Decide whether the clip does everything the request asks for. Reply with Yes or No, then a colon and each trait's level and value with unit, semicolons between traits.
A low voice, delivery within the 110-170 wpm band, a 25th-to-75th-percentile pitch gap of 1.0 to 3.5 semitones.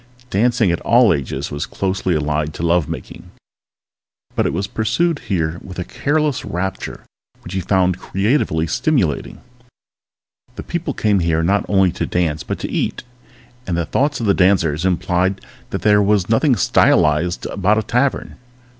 No: very low, 95 Hz; average, 155 wpm; average, 4.7 semitones